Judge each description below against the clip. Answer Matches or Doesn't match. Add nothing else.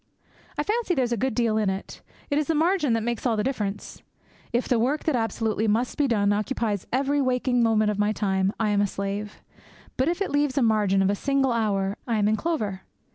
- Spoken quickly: Matches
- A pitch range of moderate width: Matches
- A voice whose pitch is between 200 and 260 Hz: Matches